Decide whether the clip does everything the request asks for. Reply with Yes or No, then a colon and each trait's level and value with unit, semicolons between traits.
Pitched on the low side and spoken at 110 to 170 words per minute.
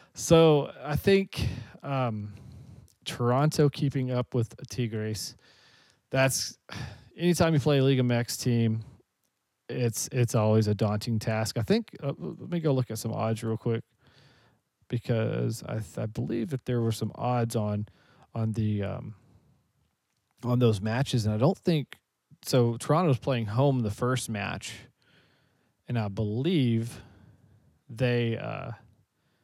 Yes: low, 120 Hz; average, 140 wpm